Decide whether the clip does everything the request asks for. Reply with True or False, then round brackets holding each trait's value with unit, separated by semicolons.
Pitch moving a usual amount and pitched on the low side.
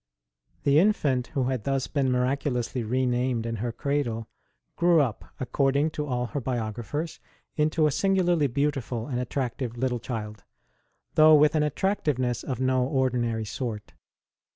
True (3.4 semitones; 130 Hz)